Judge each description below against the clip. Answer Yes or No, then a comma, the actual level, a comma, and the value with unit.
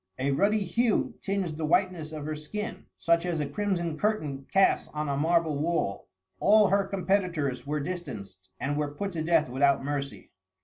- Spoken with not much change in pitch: No, average, 4.8 semitones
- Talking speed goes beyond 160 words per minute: Yes, average, 175 wpm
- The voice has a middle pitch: Yes, medium, 160 Hz